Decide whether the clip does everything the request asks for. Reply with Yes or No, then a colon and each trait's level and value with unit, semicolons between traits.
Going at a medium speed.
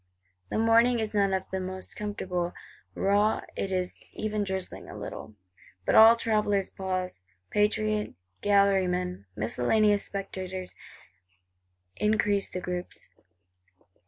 No: slow, 110 wpm